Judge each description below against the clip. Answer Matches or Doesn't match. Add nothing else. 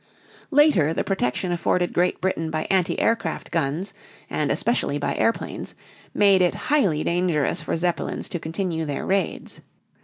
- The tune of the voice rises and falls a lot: Doesn't match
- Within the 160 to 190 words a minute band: Doesn't match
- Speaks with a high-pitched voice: Doesn't match